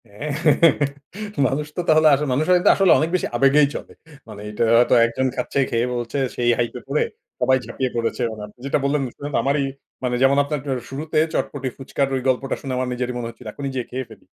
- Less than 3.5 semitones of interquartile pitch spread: Yes, average, 2.7 semitones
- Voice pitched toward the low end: Yes, low, 130 Hz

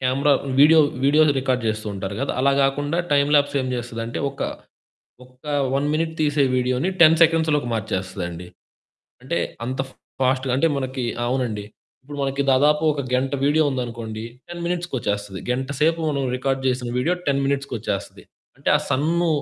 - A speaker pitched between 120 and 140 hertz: Yes, low, 135 Hz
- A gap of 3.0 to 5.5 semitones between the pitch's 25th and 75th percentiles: Yes, average, 3.3 semitones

